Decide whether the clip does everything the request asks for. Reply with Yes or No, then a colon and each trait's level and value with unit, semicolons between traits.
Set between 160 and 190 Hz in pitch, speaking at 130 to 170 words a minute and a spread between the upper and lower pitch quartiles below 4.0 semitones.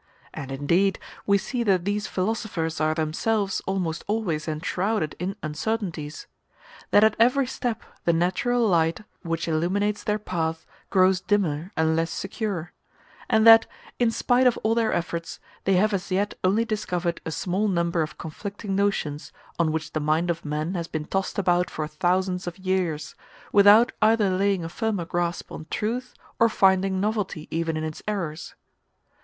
No: medium, 185 Hz; average, 160 wpm; average, 4.3 semitones